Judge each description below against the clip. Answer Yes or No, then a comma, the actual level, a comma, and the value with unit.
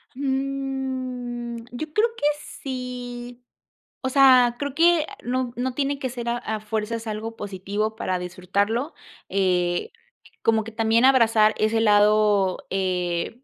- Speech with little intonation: No, average, 3.5 semitones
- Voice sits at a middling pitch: No, high, 235 Hz